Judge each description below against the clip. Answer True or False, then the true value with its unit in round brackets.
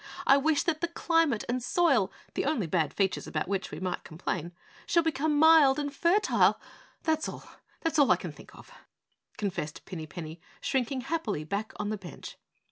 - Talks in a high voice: True (260 Hz)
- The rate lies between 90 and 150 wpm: False (180 wpm)